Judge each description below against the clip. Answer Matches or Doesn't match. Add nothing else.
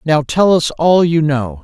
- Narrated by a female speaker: Doesn't match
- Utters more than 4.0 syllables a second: Doesn't match